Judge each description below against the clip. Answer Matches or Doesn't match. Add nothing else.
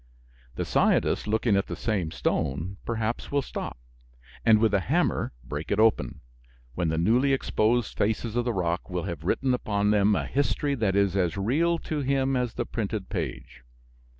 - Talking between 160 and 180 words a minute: Matches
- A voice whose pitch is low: Matches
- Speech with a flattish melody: Doesn't match